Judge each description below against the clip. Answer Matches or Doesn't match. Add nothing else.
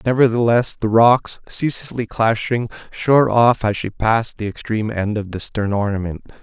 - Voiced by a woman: Doesn't match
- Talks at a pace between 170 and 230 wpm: Doesn't match